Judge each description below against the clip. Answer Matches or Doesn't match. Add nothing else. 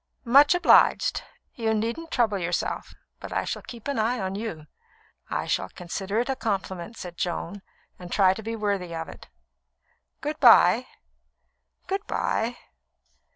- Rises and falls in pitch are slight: Doesn't match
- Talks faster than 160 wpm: Doesn't match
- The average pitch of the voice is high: Matches